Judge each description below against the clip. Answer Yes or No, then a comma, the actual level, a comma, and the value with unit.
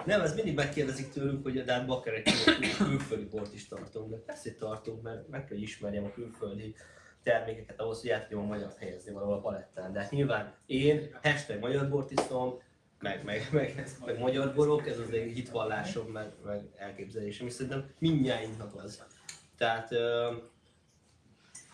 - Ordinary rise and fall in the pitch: Yes, average, 4.6 semitones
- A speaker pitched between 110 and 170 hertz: Yes, low, 115 Hz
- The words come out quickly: Yes, fast, 160 wpm